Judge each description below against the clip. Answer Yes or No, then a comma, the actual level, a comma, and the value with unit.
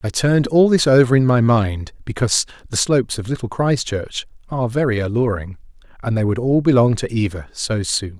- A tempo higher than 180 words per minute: Yes, average, 190 wpm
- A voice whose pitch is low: Yes, low, 120 Hz